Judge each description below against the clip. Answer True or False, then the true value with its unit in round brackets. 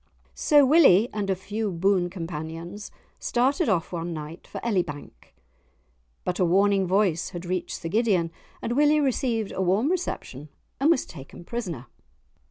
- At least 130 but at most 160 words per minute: True (150 wpm)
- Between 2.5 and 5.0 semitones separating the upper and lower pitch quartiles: False (5.5 semitones)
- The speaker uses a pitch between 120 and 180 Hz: False (190 Hz)